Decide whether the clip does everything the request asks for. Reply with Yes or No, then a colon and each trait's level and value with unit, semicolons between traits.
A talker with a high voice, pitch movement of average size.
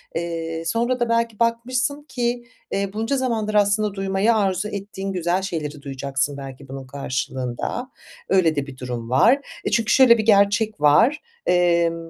No: high, 195 Hz; wide, 7.5 semitones